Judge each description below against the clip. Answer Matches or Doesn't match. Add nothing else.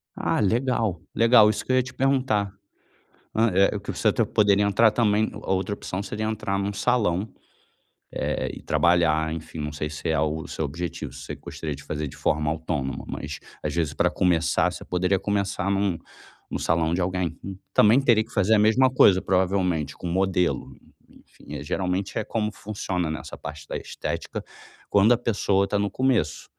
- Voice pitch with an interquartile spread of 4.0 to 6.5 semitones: Matches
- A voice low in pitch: Matches